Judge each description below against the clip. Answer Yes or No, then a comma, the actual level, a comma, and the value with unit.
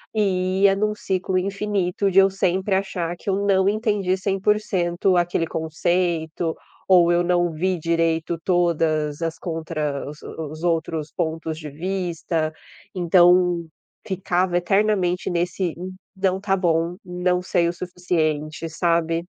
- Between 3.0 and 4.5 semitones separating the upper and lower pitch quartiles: No, narrow, 2.4 semitones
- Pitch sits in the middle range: Yes, medium, 175 Hz